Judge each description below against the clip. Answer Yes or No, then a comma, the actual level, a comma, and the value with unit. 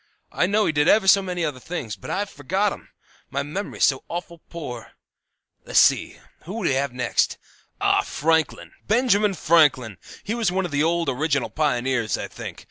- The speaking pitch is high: No, medium, 165 Hz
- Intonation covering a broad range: Yes, wide, 5.7 semitones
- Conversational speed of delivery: Yes, average, 180 wpm